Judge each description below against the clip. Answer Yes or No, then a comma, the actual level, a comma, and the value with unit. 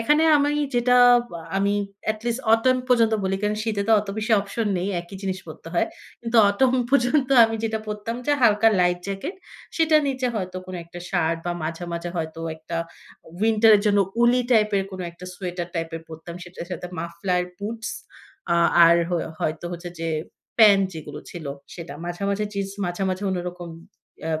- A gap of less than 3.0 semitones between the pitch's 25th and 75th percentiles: No, average, 4.5 semitones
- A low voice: No, high, 195 Hz